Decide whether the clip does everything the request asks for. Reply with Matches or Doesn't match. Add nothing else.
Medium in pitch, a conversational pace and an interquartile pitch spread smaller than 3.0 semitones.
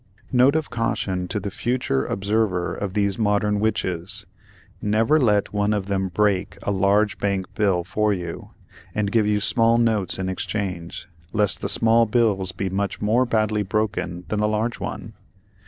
Doesn't match